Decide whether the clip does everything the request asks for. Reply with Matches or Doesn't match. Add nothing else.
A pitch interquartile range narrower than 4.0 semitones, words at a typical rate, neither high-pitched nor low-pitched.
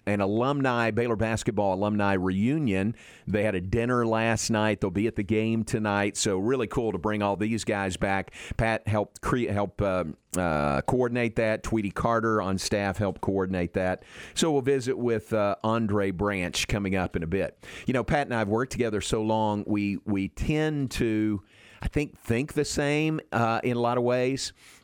Doesn't match